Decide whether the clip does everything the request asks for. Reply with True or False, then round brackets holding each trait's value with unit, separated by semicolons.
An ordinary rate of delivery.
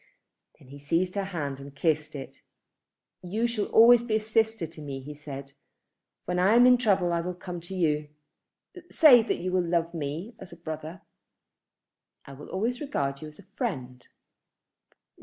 True (175 wpm)